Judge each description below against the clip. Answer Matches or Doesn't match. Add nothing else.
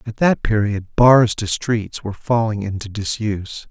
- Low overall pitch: Matches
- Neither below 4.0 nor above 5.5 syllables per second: Matches